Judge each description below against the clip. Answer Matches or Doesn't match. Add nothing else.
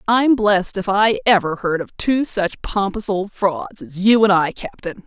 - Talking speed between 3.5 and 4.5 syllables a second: Matches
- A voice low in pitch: Doesn't match